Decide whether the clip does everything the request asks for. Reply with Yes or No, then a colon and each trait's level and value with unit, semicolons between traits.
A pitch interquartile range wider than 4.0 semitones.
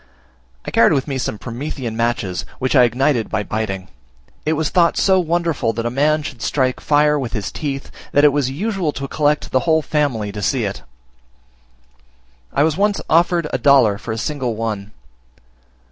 Yes: average, 4.9 semitones